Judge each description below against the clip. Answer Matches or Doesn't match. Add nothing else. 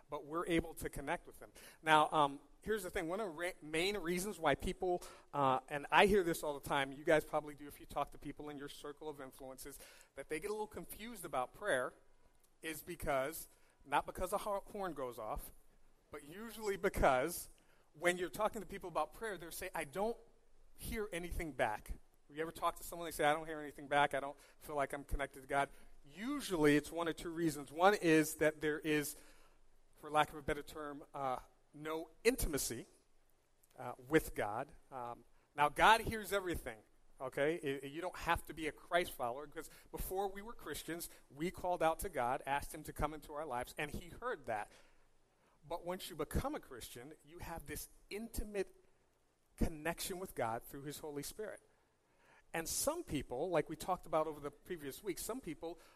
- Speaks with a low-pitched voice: Doesn't match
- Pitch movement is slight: Doesn't match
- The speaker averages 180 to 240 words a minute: Matches